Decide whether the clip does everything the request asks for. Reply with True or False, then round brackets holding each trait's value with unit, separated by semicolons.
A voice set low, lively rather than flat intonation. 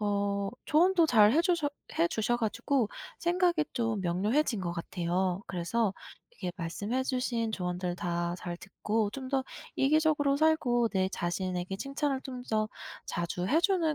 False (225 Hz; 7.3 semitones)